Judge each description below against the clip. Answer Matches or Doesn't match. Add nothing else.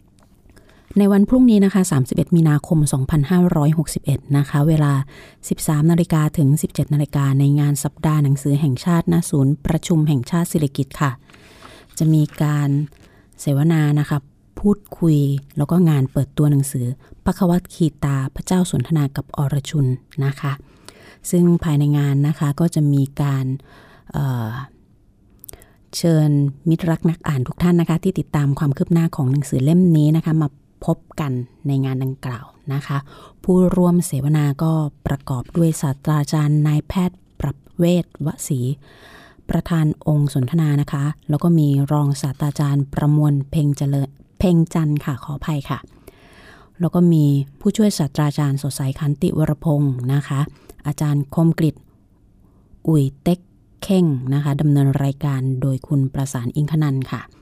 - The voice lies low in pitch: Doesn't match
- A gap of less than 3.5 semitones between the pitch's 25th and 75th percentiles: Matches